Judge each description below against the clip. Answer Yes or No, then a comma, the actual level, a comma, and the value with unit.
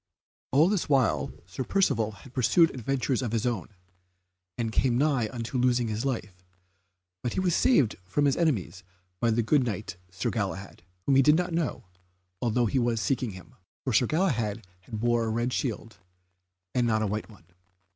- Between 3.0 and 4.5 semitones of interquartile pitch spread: Yes, average, 3.9 semitones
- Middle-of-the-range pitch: No, low, 120 Hz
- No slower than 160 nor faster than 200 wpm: Yes, average, 180 wpm